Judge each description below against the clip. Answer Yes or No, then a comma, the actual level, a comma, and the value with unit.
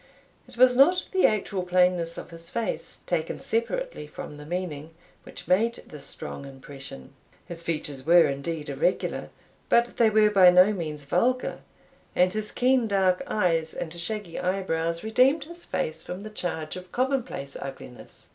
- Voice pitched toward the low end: No, medium, 180 Hz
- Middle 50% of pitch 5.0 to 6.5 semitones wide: Yes, wide, 5.5 semitones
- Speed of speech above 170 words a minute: No, average, 155 wpm